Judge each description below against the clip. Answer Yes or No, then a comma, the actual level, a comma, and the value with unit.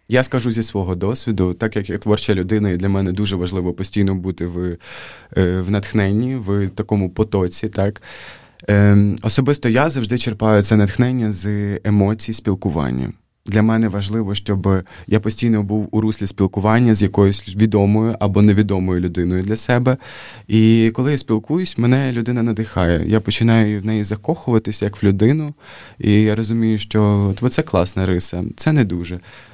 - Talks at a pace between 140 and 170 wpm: Yes, fast, 155 wpm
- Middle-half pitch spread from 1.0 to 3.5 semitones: Yes, narrow, 2.4 semitones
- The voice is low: Yes, low, 105 Hz